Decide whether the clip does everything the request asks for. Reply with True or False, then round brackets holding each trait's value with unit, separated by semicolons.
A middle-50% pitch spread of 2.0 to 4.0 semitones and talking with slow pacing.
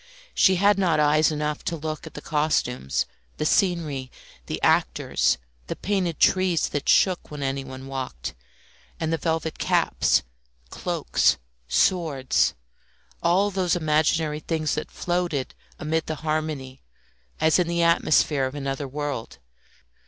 True (3.3 semitones; 130 wpm)